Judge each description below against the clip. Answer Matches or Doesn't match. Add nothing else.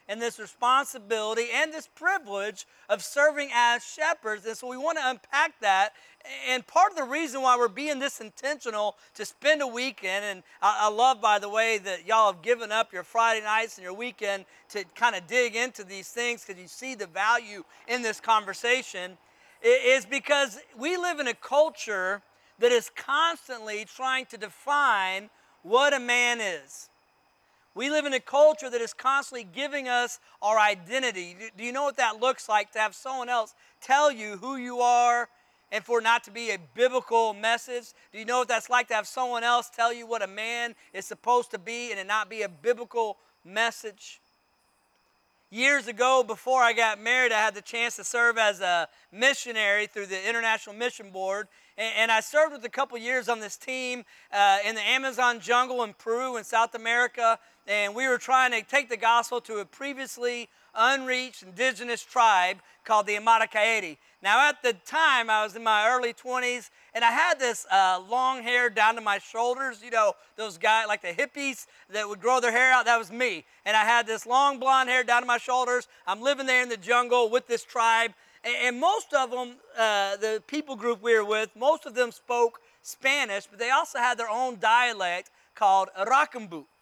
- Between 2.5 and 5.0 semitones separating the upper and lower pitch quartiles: Matches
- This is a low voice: Doesn't match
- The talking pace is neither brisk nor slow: Matches